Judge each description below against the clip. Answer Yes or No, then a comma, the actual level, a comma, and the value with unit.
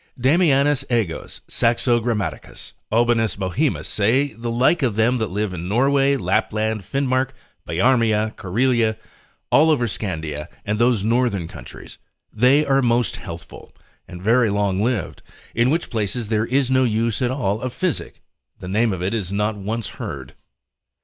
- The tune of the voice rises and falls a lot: No, average, 3.8 semitones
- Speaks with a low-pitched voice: Yes, low, 115 Hz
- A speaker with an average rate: Yes, average, 155 wpm